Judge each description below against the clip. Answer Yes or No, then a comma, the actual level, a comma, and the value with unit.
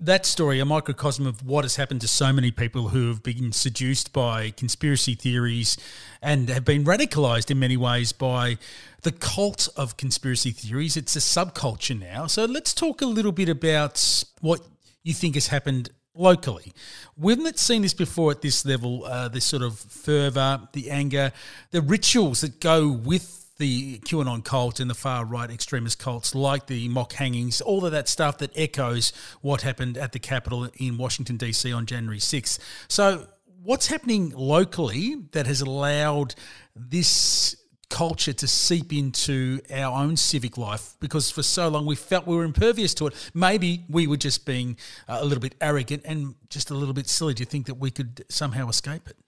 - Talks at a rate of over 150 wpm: Yes, average, 185 wpm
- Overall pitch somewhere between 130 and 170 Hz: Yes, medium, 140 Hz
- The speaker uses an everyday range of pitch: Yes, average, 4.0 semitones